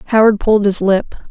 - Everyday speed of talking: Yes, average, 185 wpm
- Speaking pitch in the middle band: No, high, 205 Hz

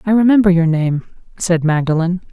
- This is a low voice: No, medium, 180 Hz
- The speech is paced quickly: No, average, 155 wpm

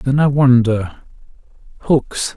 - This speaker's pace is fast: No, slow, 75 wpm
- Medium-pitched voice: No, low, 125 Hz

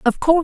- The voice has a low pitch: No, very high, 290 Hz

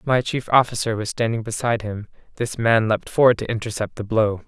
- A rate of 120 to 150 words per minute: No, average, 200 wpm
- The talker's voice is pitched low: Yes, low, 115 Hz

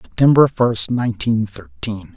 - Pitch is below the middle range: Yes, low, 120 Hz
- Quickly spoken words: No, slow, 110 wpm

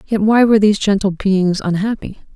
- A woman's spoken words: Yes, female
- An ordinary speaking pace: Yes, average, 180 wpm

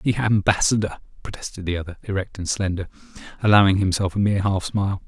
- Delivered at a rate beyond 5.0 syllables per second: Yes, 6.4 syllables/s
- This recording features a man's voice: Yes, male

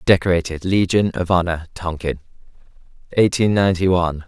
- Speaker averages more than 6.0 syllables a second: No, 5.7 syllables/s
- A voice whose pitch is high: No, very low, 90 Hz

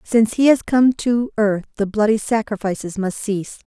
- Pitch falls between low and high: No, high, 220 Hz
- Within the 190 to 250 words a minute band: No, average, 180 wpm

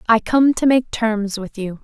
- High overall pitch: Yes, high, 225 Hz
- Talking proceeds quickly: Yes, fast, 230 wpm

